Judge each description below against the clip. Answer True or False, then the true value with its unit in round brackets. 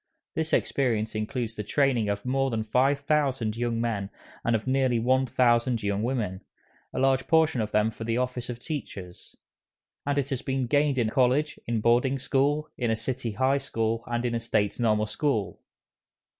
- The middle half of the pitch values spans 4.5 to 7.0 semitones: False (3.3 semitones)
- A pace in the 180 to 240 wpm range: True (185 wpm)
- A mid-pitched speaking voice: False (120 Hz)